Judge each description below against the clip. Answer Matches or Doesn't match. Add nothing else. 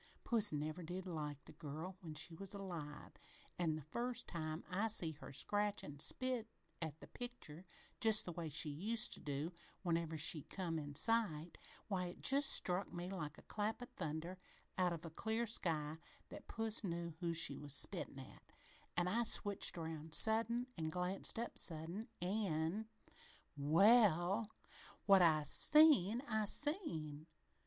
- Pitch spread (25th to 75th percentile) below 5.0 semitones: Doesn't match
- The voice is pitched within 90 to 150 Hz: Doesn't match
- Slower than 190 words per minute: Matches